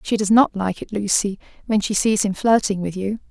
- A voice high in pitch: Yes, high, 205 Hz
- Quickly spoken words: Yes, fast, 235 wpm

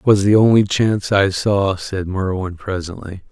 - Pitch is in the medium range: No, very low, 95 Hz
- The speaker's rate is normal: Yes, average, 165 wpm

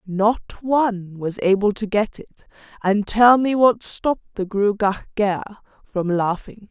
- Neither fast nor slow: Yes, average, 150 wpm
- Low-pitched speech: No, high, 210 Hz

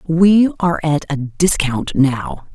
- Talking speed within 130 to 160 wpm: Yes, average, 140 wpm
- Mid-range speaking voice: Yes, medium, 160 Hz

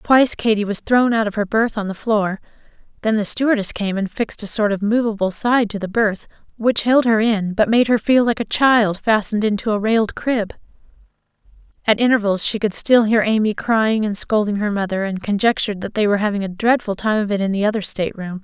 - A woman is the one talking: Yes, female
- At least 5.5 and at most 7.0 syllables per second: Yes, 5.8 syllables/s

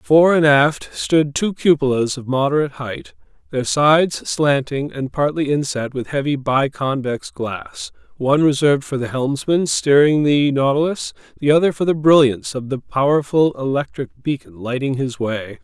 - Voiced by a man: Yes, male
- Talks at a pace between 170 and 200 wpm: No, average, 155 wpm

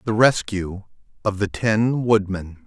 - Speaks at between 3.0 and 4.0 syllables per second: Yes, 3.7 syllables/s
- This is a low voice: Yes, low, 105 Hz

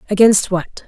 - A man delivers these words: No, female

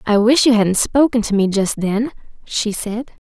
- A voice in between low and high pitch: No, high, 220 Hz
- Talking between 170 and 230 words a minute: Yes, average, 200 wpm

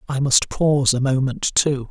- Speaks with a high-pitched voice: No, low, 135 Hz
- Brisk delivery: No, average, 190 wpm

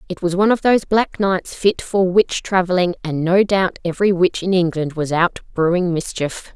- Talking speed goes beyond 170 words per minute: Yes, average, 200 wpm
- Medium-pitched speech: Yes, medium, 180 Hz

